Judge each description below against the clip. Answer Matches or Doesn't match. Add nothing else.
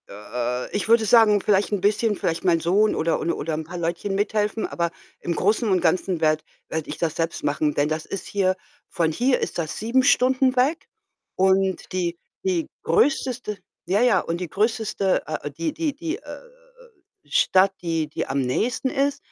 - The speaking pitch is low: Doesn't match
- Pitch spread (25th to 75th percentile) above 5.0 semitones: Matches